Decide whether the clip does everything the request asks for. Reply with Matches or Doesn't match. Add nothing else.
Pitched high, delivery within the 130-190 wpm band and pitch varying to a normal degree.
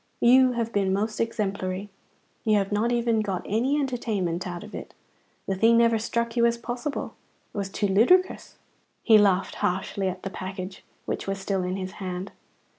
Matches